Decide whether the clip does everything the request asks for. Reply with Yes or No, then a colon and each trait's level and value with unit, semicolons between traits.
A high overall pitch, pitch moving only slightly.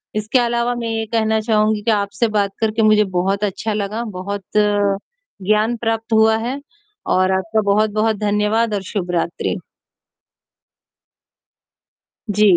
Yes: high, 215 Hz; narrow, 1.7 semitones